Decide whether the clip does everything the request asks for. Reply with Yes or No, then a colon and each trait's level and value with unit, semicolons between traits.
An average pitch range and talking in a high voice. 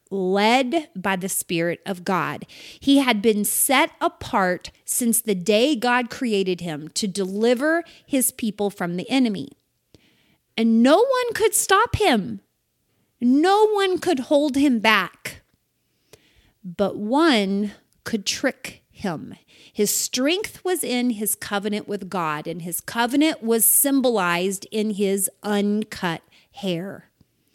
No: wide, 5.7 semitones; high, 220 Hz